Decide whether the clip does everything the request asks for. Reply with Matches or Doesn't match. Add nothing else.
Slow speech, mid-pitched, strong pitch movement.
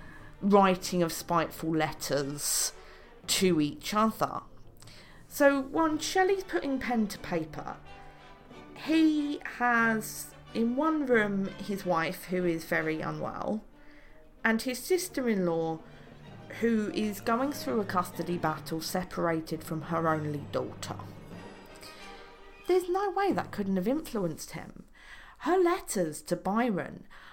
Doesn't match